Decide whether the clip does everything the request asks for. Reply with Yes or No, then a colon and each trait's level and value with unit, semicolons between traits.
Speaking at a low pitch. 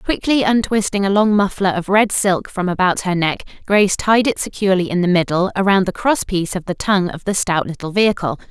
No: high, 190 Hz